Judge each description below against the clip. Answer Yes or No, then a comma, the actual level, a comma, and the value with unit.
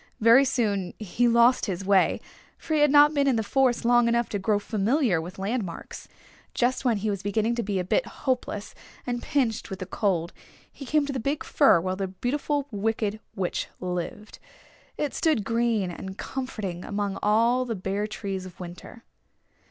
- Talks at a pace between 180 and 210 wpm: Yes, average, 185 wpm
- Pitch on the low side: No, high, 220 Hz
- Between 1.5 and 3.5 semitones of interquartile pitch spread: No, average, 4.4 semitones